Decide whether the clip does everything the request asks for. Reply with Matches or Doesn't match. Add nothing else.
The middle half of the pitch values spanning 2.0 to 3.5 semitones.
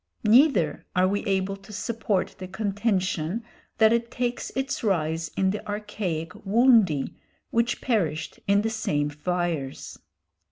Doesn't match